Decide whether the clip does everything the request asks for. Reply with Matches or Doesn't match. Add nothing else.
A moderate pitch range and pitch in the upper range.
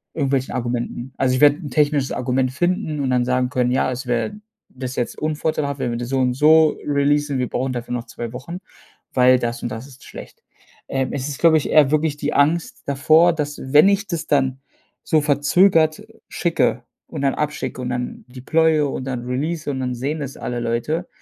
Doesn't match